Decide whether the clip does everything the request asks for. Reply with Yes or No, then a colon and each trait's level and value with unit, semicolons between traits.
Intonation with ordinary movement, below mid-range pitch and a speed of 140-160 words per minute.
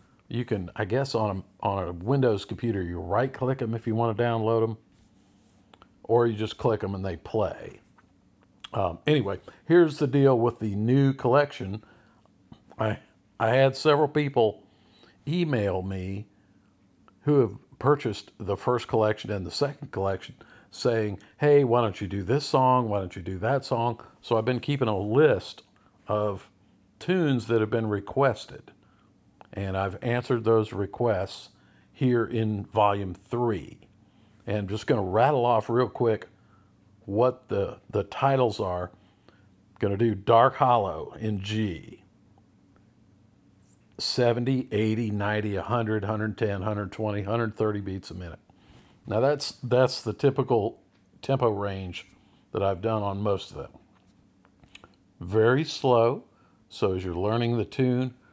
Yes: average, 3.8 semitones; low, 110 Hz; average, 145 wpm